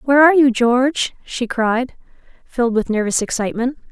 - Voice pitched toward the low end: No, high, 245 Hz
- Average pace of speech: Yes, average, 155 wpm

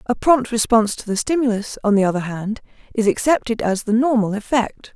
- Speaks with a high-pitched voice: Yes, high, 225 Hz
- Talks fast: No, average, 195 wpm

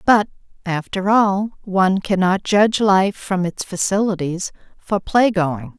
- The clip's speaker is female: Yes, female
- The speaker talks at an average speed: No, slow, 125 wpm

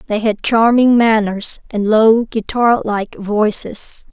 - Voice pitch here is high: Yes, high, 220 Hz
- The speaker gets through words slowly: Yes, slow, 130 wpm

